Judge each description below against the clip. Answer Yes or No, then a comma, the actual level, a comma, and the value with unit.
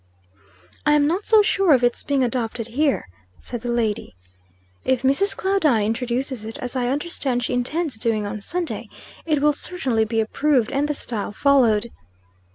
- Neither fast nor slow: Yes, average, 165 wpm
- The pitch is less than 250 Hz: No, very high, 255 Hz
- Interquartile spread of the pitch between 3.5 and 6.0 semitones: Yes, average, 4.5 semitones